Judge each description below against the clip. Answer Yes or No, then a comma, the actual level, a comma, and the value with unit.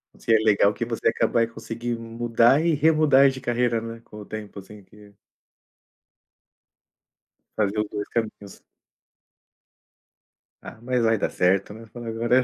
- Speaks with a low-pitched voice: Yes, low, 115 Hz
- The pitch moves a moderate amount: No, narrow, 2.2 semitones